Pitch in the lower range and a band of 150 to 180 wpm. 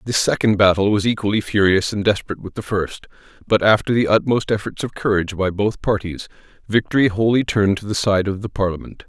No: low, 105 Hz; average, 200 wpm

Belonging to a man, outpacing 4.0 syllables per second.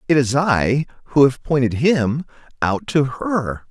No: male; 3.9 syllables/s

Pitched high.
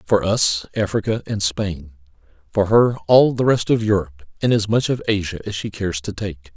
No: low, 100 Hz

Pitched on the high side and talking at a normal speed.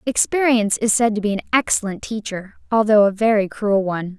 Yes: high, 215 Hz; average, 185 wpm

